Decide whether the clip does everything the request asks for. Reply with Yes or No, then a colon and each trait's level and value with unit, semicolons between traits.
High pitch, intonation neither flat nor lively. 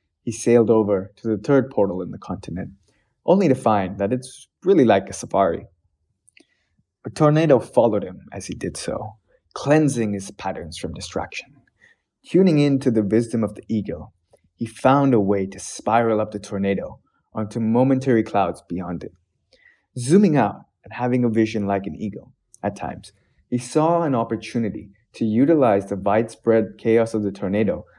No: low, 110 Hz; average, 3.7 semitones